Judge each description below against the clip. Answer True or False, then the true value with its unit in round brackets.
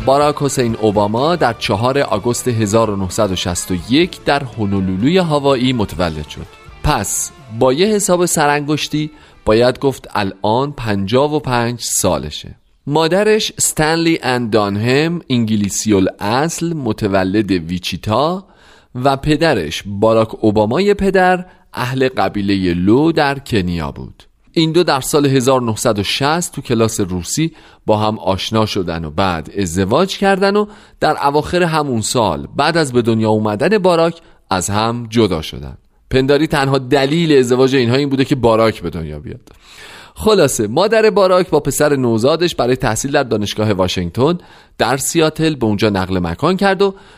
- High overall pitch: False (125 Hz)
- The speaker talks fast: False (130 wpm)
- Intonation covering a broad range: True (6.8 semitones)